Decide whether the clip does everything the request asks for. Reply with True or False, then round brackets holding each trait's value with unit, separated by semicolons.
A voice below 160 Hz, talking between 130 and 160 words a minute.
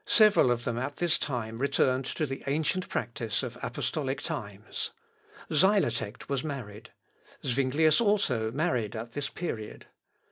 True (135 Hz; 135 wpm)